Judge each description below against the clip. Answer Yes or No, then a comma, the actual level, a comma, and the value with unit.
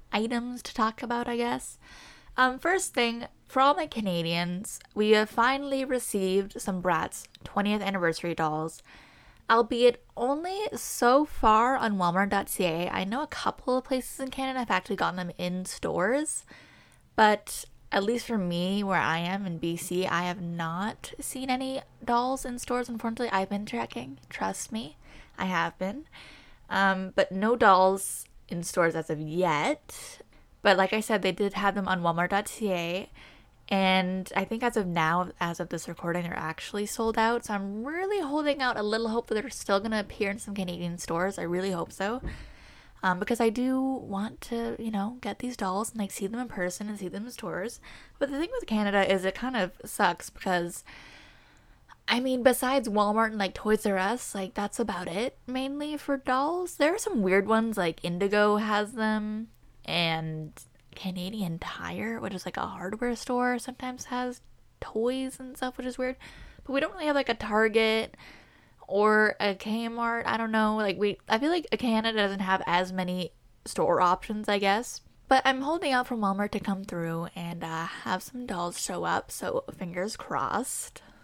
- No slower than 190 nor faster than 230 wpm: No, average, 180 wpm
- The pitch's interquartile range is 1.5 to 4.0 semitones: No, average, 4.9 semitones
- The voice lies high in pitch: Yes, high, 210 Hz